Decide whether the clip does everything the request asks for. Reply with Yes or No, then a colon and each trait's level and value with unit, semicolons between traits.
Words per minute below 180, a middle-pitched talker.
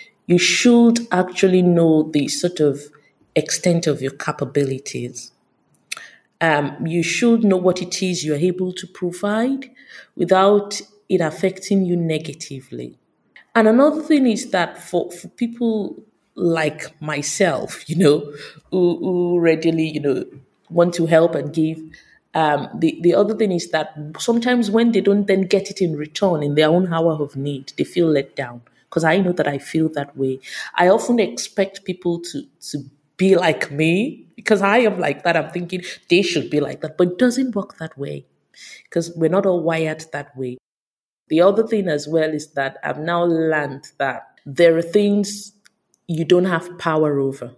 Yes: average, 170 wpm; medium, 170 Hz